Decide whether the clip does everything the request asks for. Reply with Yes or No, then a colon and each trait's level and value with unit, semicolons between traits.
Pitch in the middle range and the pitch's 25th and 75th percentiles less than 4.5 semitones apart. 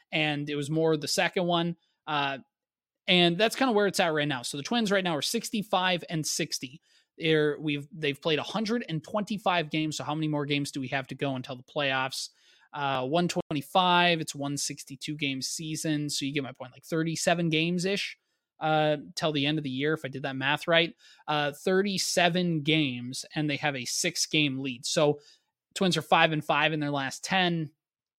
Yes: medium, 155 Hz; average, 3.4 semitones